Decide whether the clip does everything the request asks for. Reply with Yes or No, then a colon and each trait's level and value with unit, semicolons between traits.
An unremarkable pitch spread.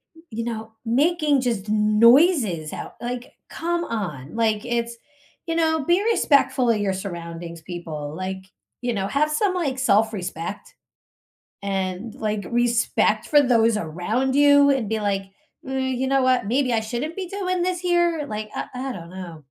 No: wide, 6.1 semitones